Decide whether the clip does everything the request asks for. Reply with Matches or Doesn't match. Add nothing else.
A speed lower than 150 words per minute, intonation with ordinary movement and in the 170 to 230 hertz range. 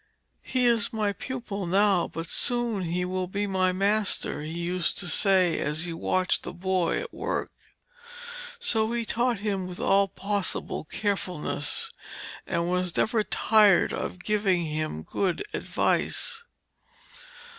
Matches